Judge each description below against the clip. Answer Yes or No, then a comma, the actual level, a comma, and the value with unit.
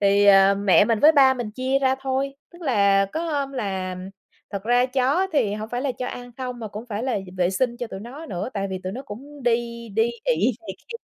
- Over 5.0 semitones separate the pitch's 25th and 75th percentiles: No, average, 4.6 semitones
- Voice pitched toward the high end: Yes, high, 240 Hz